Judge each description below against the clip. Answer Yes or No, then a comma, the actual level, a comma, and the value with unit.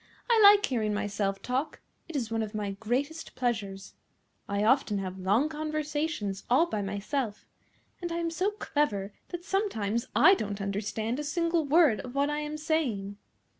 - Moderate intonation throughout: No, wide, 7.3 semitones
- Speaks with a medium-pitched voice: No, very high, 250 Hz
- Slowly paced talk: No, average, 170 wpm